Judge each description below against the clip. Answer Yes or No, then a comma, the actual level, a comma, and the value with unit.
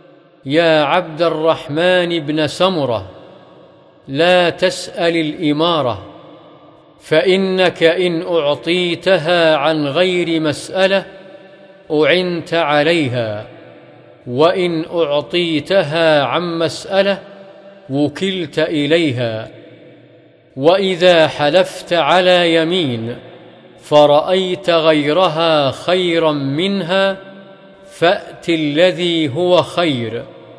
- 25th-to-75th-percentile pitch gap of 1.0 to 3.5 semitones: Yes, average, 2.7 semitones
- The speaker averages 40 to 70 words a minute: Yes, slow, 65 wpm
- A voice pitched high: No, medium, 170 Hz